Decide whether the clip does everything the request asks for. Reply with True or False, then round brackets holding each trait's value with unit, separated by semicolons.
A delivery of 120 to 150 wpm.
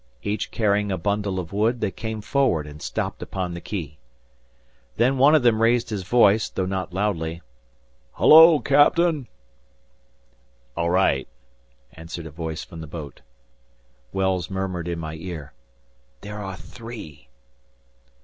True (140 wpm)